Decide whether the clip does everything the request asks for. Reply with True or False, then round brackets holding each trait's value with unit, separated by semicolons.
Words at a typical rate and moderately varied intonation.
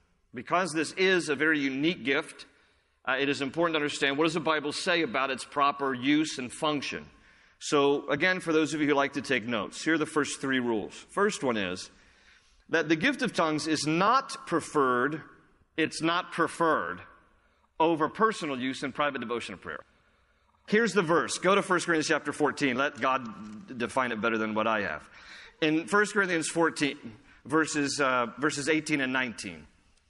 True (180 wpm; 3.8 semitones)